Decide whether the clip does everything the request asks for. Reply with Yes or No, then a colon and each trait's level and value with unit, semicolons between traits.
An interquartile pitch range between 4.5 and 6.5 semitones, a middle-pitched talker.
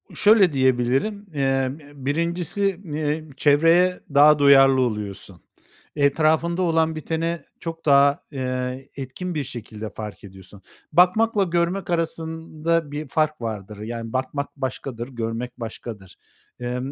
Yes: average, 5.1 semitones; medium, 145 Hz